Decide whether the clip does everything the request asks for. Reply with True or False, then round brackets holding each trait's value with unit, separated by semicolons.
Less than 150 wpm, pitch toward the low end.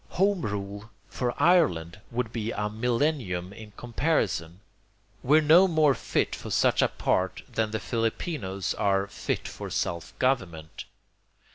True (135 wpm; 110 Hz)